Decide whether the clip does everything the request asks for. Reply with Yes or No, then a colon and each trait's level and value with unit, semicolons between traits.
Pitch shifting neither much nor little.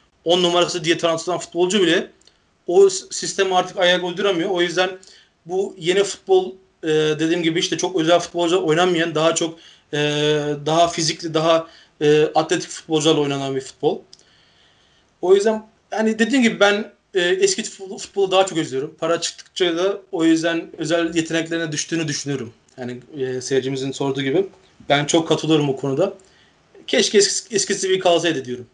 Yes: average, 3.3 semitones